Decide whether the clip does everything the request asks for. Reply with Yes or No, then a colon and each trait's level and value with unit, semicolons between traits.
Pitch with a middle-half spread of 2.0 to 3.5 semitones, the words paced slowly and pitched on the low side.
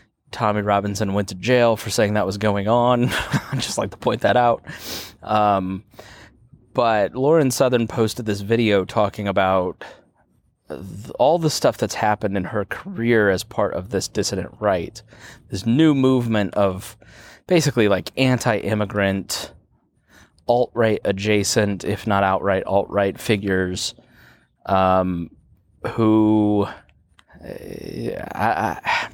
Yes: average, 2.9 semitones; slow, 125 wpm; low, 105 Hz